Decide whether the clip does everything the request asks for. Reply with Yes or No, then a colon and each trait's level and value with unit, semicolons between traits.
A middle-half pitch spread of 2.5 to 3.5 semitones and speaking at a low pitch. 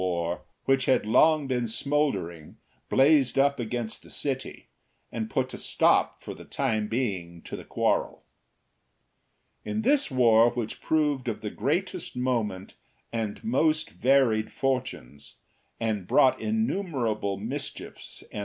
No: average, 4.5 semitones; low, 125 Hz